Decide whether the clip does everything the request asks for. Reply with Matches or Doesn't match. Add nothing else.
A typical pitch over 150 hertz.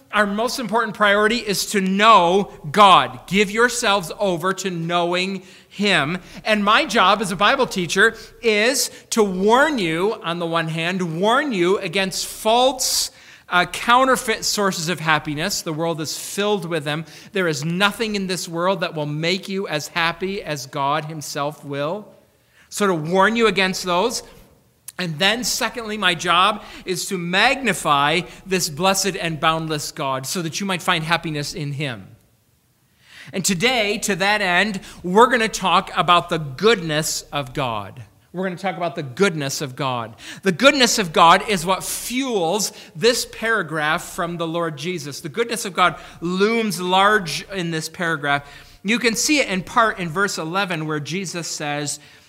Matches